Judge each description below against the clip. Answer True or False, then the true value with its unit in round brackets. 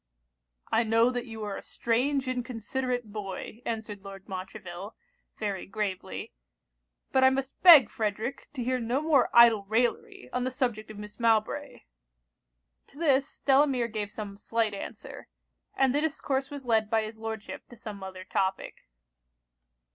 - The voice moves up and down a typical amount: True (3.6 semitones)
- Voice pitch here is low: False (225 Hz)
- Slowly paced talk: False (150 wpm)